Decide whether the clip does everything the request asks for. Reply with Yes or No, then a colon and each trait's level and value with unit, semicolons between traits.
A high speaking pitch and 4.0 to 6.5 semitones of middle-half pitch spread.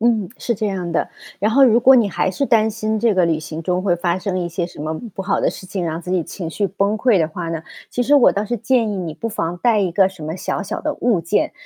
Yes: high, 195 Hz; average, 4.3 semitones